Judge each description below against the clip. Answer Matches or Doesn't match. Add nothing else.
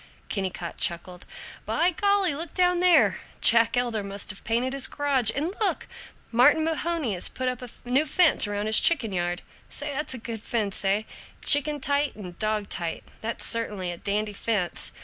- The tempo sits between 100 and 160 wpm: Doesn't match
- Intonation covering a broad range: Matches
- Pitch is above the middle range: Matches